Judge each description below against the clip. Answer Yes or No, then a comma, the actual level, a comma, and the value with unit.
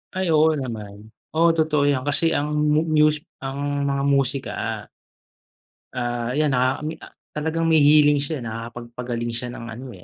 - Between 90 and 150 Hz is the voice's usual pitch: Yes, medium, 140 Hz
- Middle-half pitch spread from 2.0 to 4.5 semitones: Yes, average, 4.0 semitones